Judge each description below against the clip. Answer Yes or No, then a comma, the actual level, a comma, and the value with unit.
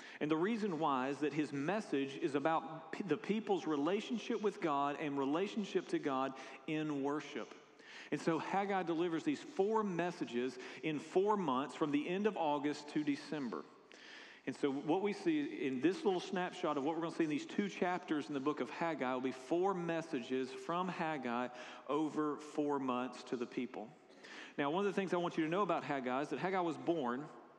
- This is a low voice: No, medium, 160 Hz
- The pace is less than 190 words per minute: No, average, 200 wpm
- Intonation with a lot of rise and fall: Yes, wide, 5.7 semitones